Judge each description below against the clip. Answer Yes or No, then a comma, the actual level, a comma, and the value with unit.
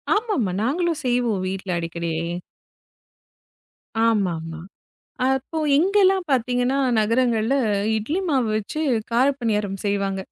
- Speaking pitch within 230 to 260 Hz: Yes, high, 235 Hz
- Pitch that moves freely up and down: Yes, wide, 5.7 semitones